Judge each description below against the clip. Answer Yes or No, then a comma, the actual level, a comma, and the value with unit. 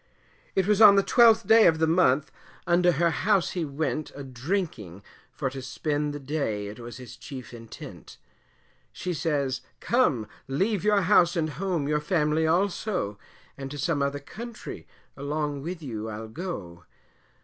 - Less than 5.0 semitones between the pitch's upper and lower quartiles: No, wide, 5.6 semitones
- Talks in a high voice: No, medium, 150 Hz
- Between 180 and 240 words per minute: No, average, 160 wpm